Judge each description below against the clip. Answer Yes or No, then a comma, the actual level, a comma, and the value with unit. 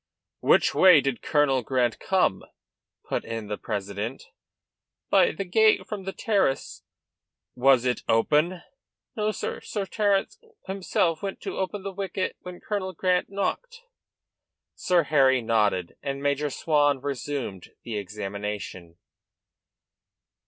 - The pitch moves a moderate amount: No, wide, 8.7 semitones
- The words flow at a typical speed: No, slow, 125 wpm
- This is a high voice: No, medium, 145 Hz